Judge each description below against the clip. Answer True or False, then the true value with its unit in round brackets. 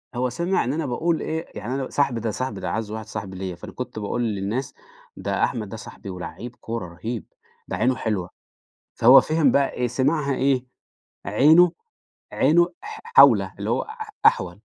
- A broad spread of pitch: True (6.0 semitones)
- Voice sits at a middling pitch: False (125 Hz)